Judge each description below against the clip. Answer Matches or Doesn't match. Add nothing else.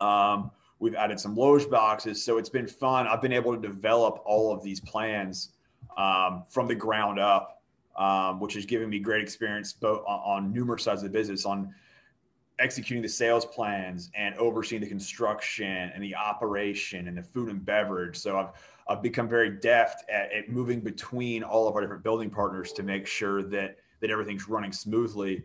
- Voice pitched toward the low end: Matches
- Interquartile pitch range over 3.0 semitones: Doesn't match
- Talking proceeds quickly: Doesn't match